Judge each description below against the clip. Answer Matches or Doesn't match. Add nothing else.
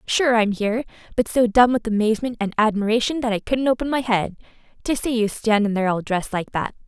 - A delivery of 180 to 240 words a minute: Matches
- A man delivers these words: Doesn't match